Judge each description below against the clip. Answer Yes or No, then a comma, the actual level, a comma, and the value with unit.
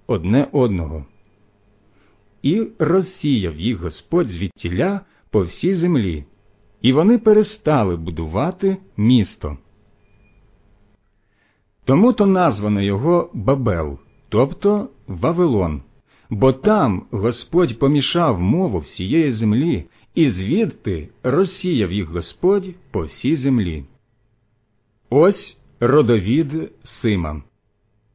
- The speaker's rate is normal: No, slow, 85 wpm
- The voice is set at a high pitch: No, low, 115 Hz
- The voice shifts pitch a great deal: Yes, wide, 8.2 semitones